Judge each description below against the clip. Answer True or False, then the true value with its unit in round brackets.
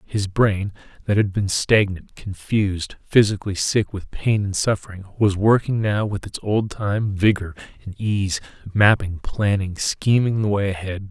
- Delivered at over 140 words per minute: True (155 wpm)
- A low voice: True (100 Hz)